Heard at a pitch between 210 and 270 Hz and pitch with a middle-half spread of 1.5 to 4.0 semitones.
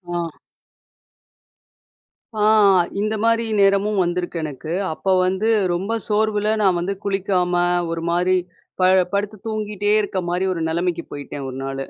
No: medium, 185 Hz; average, 3.2 semitones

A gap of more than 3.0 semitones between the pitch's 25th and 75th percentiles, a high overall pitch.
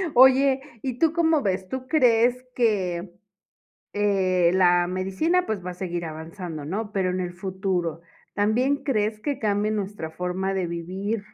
Yes: average, 4.9 semitones; high, 195 Hz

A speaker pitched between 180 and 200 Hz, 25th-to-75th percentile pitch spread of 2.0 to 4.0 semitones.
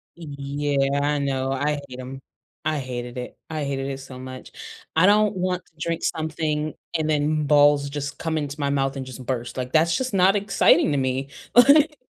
No: medium, 145 Hz; average, 2.9 semitones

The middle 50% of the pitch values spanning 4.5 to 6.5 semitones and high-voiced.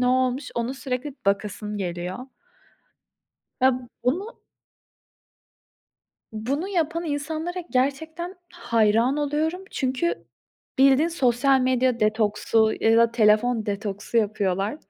Yes: average, 5.3 semitones; very high, 255 Hz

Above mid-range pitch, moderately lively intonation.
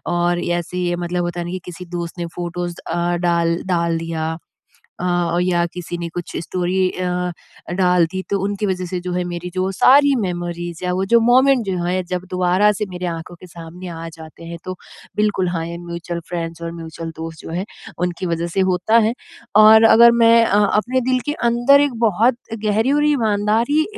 No: medium, 180 Hz; average, 3.3 semitones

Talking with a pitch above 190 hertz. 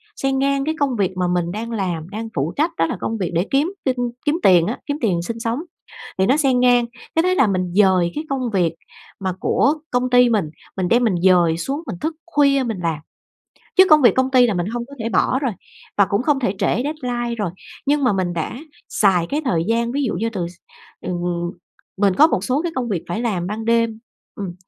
Yes: high, 230 Hz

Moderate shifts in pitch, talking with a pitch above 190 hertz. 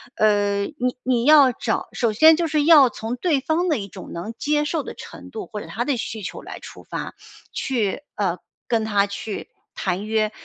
No: wide, 6.1 semitones; high, 235 Hz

